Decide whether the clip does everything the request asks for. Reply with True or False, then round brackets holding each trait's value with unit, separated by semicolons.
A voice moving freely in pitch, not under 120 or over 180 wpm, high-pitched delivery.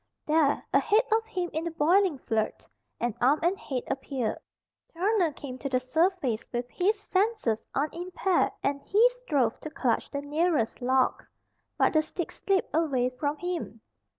True (6.0 semitones; 155 wpm; 310 Hz)